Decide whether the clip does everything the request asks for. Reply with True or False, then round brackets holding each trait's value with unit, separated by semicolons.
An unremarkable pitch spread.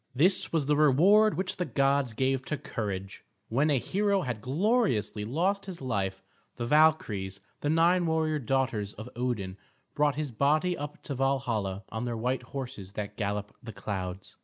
False (6.6 semitones)